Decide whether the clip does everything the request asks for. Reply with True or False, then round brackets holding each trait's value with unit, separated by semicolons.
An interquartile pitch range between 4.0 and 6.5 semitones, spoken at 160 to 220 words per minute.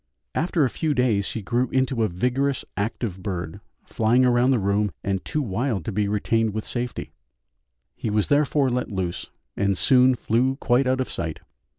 True (4.4 semitones; 180 wpm)